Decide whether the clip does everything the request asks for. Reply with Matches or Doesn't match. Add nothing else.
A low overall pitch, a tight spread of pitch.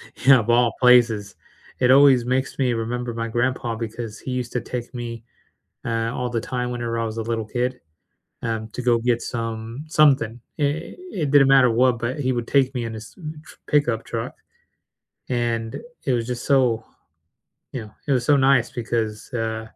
Matches